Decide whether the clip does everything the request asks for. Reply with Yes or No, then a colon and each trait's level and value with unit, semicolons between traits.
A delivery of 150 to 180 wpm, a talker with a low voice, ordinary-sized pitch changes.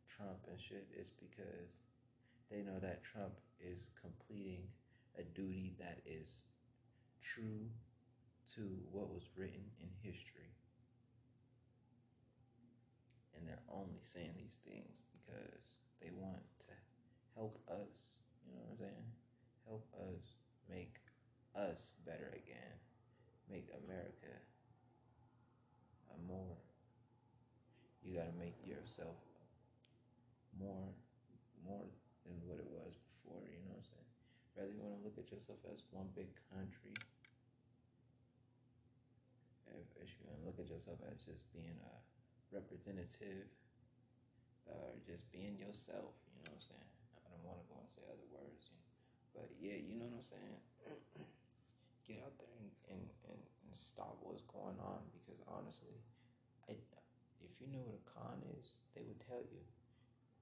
No: average, 140 wpm; low, 120 Hz; average, 3.5 semitones